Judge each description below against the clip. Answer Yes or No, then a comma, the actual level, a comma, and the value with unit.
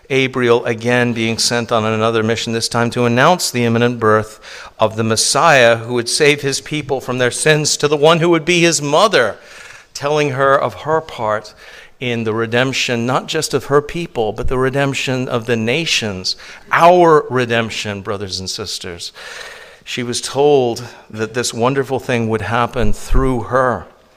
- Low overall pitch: Yes, low, 125 Hz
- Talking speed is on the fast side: No, average, 170 wpm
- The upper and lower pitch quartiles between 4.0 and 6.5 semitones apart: No, average, 3.5 semitones